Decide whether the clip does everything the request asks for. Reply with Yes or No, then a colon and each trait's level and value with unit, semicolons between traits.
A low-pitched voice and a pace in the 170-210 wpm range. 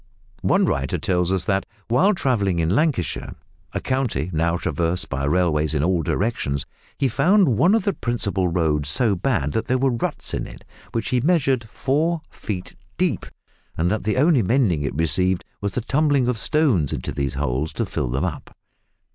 Yes: low, 100 Hz; average, 180 wpm